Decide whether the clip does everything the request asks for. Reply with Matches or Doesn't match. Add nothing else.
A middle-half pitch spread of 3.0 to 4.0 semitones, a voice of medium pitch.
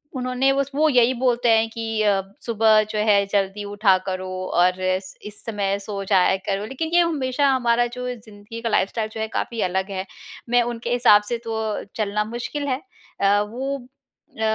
Doesn't match